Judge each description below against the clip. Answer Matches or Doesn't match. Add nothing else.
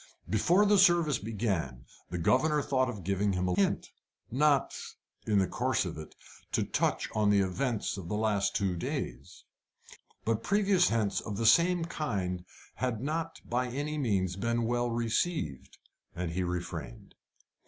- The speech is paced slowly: Doesn't match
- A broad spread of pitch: Matches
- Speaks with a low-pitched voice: Matches